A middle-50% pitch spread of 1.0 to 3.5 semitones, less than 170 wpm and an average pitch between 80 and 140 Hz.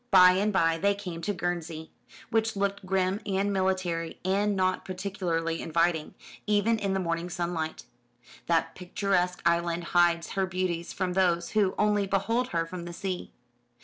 No: narrow, 2.6 semitones; average, 155 wpm; medium, 185 Hz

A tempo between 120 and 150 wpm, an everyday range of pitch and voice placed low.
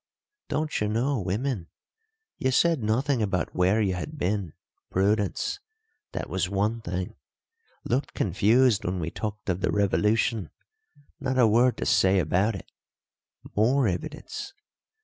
Yes: slow, 135 wpm; average, 4.8 semitones; low, 105 Hz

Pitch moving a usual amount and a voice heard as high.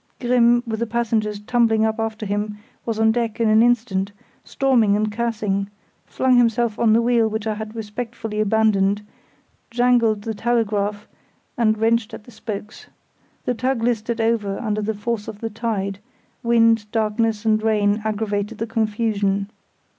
No: narrow, 1.9 semitones; high, 220 Hz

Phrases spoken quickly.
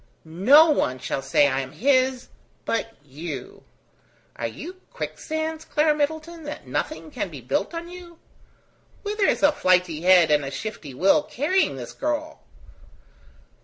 No: average, 145 wpm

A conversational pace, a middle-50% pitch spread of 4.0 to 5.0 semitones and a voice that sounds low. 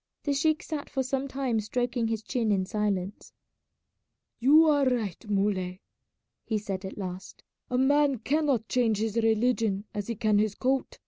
No: average, 165 wpm; average, 4.3 semitones; high, 225 Hz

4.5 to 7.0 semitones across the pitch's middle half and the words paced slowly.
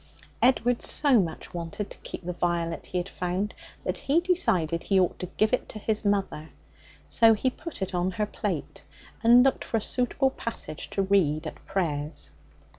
No: average, 5.2 semitones; average, 185 wpm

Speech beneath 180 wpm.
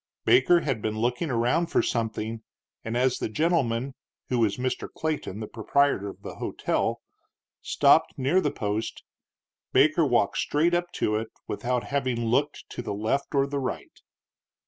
Yes: average, 160 wpm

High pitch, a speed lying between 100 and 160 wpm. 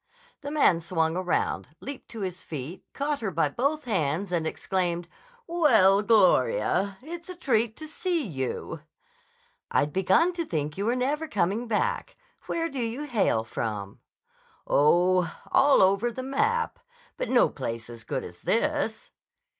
Yes: high, 215 Hz; average, 150 wpm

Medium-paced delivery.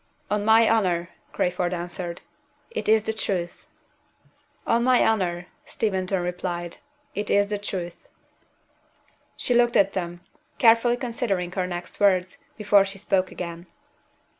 No: slow, 130 wpm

